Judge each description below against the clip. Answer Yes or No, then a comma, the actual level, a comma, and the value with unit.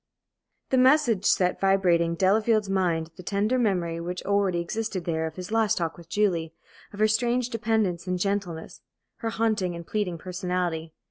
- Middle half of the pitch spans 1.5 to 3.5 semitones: No, average, 4.0 semitones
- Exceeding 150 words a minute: Yes, average, 170 wpm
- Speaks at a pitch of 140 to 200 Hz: Yes, high, 190 Hz